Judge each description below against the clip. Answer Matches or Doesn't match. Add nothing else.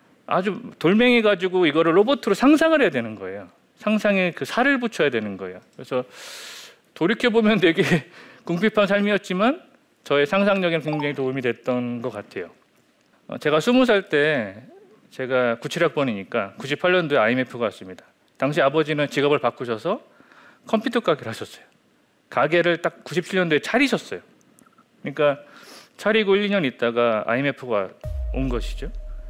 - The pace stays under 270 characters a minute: Doesn't match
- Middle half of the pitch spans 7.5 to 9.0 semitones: Matches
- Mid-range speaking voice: Matches